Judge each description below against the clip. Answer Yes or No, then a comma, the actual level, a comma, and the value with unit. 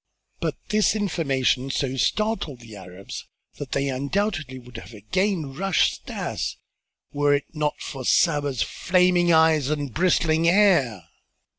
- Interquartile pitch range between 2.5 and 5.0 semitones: No, wide, 5.5 semitones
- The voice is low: No, medium, 150 Hz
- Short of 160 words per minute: Yes, slow, 135 wpm